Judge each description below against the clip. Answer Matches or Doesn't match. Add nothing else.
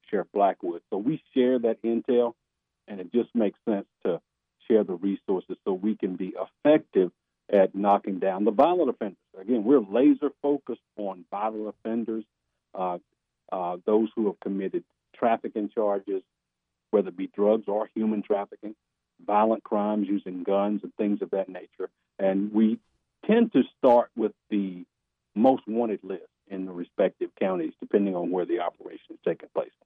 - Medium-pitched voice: Doesn't match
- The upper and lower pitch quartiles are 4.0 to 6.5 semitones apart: Matches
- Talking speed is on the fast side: Doesn't match